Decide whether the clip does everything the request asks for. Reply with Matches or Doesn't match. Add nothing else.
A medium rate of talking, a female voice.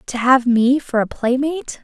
Matches